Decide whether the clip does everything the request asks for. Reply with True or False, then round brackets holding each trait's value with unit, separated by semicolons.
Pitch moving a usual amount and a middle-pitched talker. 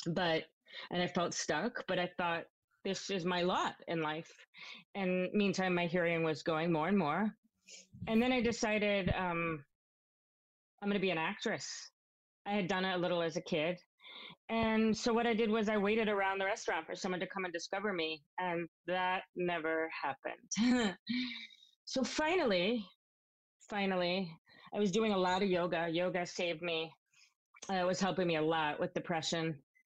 True (3.5 semitones; 180 Hz)